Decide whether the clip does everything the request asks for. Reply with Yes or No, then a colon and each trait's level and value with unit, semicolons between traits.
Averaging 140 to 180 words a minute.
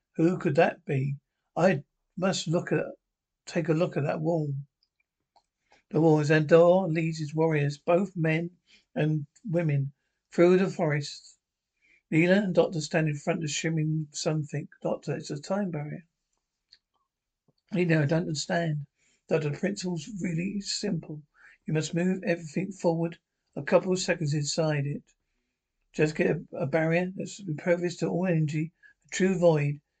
Yes: average, 155 wpm